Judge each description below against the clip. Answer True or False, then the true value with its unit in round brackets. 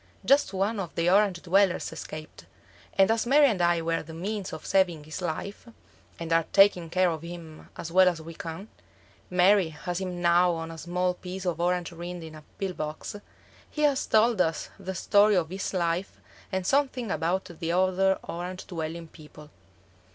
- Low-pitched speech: False (180 Hz)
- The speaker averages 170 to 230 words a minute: True (185 wpm)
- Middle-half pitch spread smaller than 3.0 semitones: True (2.6 semitones)